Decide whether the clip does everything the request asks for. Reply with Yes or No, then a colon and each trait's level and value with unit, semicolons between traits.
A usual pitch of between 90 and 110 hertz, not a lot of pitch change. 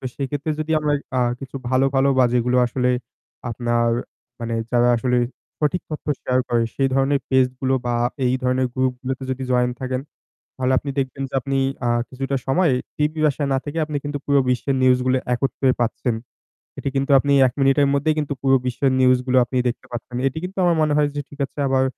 No: low, 135 Hz; narrow, 2.0 semitones